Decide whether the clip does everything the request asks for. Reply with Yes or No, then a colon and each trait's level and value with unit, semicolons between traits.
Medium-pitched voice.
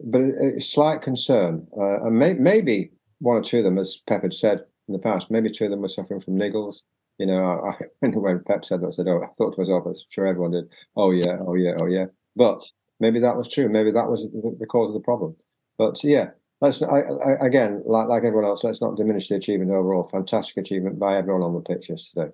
No: low, 105 Hz